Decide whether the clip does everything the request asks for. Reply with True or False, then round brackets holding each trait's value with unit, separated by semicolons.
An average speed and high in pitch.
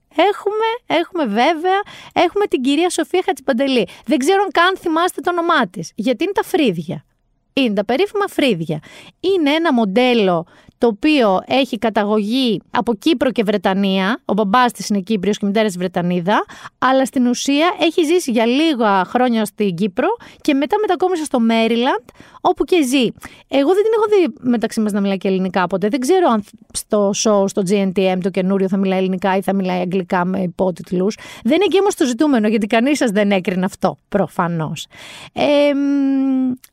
False (175 wpm; 245 Hz)